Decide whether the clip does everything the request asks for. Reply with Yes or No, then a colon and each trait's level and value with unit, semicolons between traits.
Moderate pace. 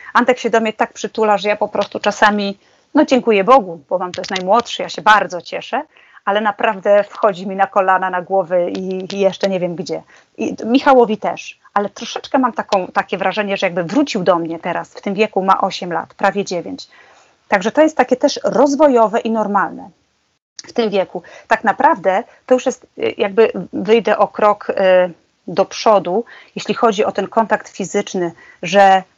No: fast, 185 wpm